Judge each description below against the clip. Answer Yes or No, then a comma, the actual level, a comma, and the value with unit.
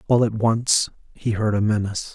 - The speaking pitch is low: Yes, low, 110 Hz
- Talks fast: No, average, 195 wpm